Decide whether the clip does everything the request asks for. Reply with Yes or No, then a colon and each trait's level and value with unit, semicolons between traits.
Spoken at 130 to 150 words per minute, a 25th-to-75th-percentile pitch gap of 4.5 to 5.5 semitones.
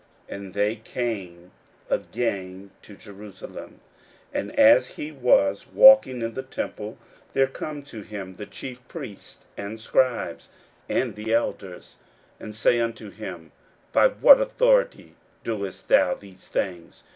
Yes: average, 140 wpm; average, 4.8 semitones